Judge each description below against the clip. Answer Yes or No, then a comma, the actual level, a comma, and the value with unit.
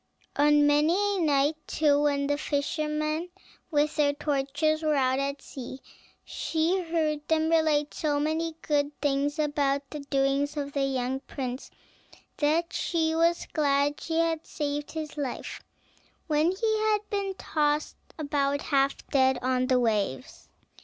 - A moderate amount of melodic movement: No, narrow, 2.2 semitones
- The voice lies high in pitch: Yes, very high, 295 Hz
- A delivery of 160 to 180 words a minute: No, average, 145 wpm